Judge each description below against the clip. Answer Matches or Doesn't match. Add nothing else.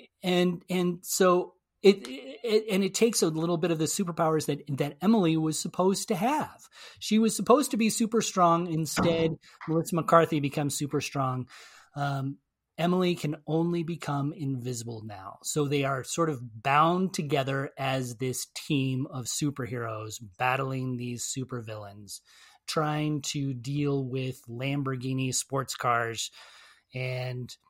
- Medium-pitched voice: Matches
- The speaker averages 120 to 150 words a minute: Matches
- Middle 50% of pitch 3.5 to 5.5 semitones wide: Matches